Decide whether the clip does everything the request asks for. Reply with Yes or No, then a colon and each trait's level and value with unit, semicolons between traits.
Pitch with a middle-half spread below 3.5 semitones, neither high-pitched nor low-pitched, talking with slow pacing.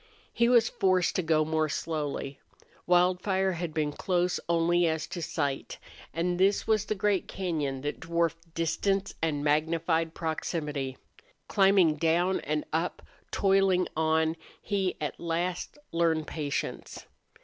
Yes: average, 2.7 semitones; medium, 165 Hz; slow, 130 wpm